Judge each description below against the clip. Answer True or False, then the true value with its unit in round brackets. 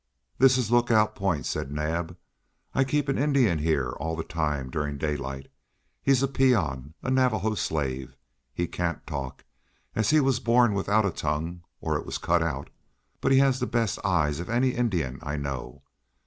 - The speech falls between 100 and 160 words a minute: False (175 wpm)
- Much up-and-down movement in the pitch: True (8.6 semitones)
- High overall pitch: False (85 Hz)